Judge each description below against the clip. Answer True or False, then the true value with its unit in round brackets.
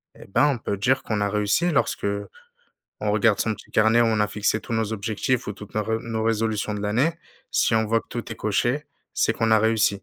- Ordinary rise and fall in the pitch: False (1.5 semitones)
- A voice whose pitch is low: True (110 Hz)